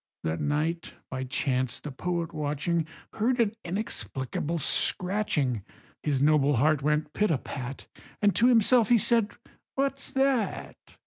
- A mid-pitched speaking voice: Yes, medium, 160 Hz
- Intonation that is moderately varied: No, wide, 7.0 semitones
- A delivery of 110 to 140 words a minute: Yes, slow, 135 wpm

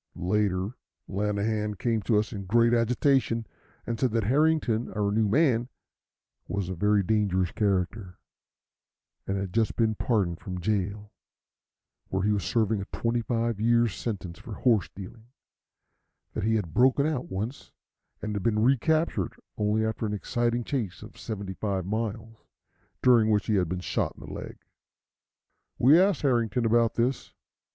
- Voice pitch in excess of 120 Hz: No, low, 110 Hz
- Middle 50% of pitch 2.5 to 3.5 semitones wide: Yes, average, 2.9 semitones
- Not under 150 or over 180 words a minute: Yes, average, 155 wpm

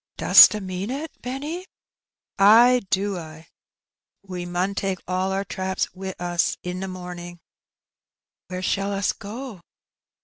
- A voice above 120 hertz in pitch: Yes, high, 190 Hz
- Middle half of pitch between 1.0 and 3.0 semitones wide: Yes, narrow, 2.5 semitones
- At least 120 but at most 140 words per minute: Yes, slow, 135 wpm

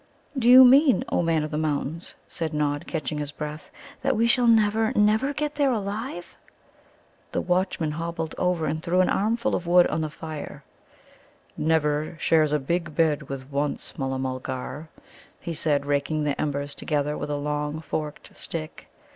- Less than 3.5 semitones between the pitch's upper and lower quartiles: No, average, 3.9 semitones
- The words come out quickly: No, average, 170 wpm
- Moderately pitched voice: Yes, medium, 155 Hz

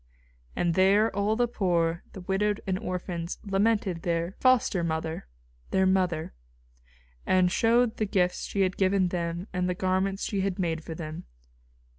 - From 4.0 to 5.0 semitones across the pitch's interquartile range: No, narrow, 2.6 semitones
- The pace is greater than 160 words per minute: No, average, 155 wpm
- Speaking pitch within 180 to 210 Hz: Yes, medium, 185 Hz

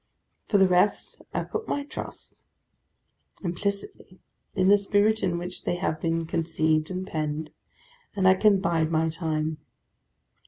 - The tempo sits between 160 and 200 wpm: No, average, 145 wpm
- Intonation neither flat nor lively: Yes, average, 3.6 semitones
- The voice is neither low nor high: Yes, medium, 175 Hz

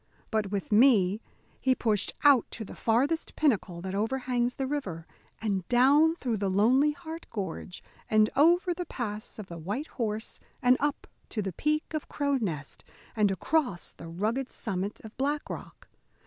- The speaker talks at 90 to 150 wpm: No, average, 165 wpm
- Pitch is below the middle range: No, high, 230 Hz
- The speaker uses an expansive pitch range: Yes, wide, 5.9 semitones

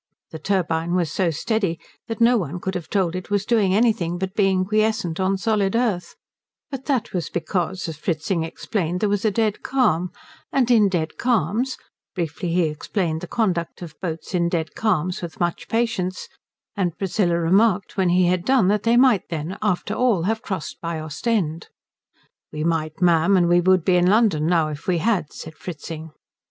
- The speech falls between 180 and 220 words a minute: Yes, average, 185 wpm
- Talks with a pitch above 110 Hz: Yes, medium, 185 Hz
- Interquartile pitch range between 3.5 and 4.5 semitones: Yes, average, 4.2 semitones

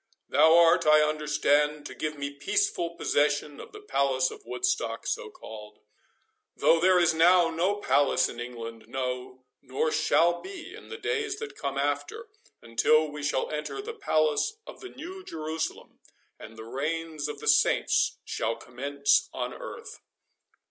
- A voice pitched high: No, medium, 150 Hz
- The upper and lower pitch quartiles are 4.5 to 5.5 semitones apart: Yes, average, 4.8 semitones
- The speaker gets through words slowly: No, average, 155 wpm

